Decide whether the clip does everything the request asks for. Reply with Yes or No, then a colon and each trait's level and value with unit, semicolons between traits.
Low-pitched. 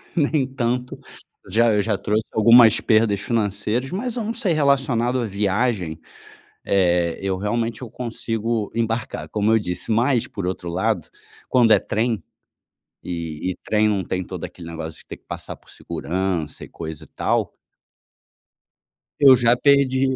Yes: low, 110 Hz